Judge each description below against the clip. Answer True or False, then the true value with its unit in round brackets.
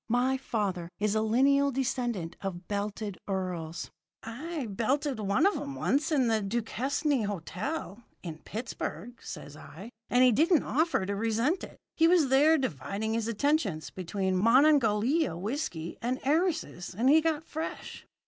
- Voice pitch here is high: True (230 Hz)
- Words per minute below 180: True (150 wpm)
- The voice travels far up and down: True (6.1 semitones)